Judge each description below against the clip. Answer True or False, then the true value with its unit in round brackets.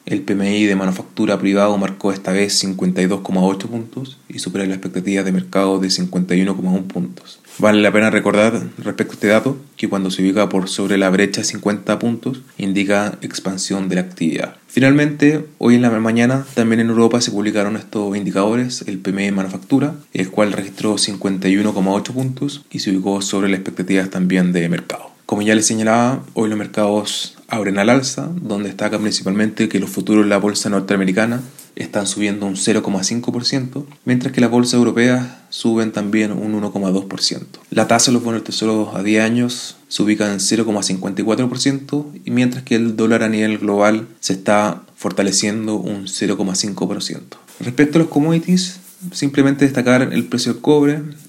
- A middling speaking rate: True (165 wpm)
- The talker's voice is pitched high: False (105 Hz)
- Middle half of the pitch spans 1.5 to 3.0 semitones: False (3.6 semitones)